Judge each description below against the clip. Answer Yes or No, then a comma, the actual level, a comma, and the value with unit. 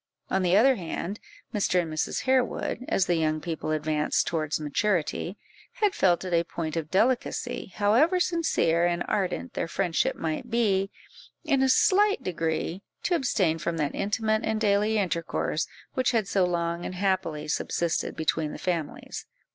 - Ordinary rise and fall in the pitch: Yes, average, 5.0 semitones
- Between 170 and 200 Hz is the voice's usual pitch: Yes, medium, 185 Hz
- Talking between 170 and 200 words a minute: No, average, 160 wpm